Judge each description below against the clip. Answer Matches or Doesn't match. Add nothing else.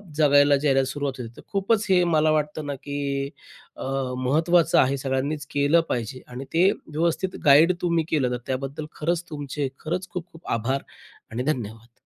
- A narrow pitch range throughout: Doesn't match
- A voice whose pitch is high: Doesn't match